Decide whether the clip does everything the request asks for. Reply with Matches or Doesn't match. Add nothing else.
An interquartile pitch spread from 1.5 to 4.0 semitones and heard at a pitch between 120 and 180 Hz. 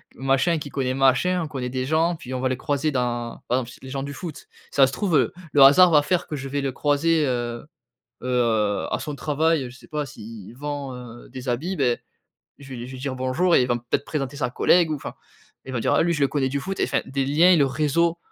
Matches